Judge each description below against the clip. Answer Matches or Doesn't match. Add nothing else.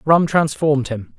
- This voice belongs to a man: Matches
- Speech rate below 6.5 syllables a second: Matches